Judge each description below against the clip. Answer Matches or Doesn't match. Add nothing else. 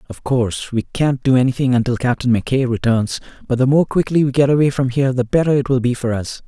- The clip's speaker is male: Matches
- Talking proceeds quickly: Matches